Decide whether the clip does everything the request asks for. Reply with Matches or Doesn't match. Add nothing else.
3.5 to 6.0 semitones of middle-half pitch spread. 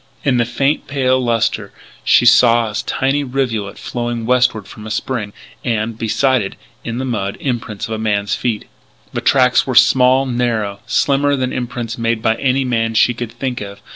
Doesn't match